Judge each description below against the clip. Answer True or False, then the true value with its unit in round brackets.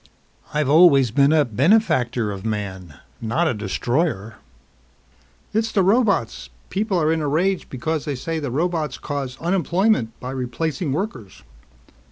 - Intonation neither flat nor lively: False (6.5 semitones)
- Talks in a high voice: False (145 Hz)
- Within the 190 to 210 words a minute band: False (140 wpm)